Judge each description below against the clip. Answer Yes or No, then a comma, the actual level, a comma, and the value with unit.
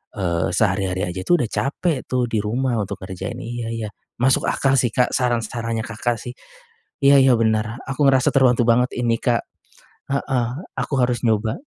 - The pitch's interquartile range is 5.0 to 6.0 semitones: No, average, 2.8 semitones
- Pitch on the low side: Yes, low, 120 Hz